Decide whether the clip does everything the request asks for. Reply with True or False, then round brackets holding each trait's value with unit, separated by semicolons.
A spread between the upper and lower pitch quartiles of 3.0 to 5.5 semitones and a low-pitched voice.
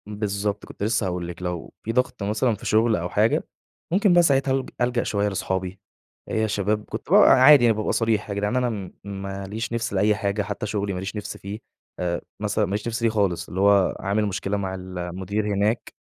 False (2.4 semitones; 105 Hz)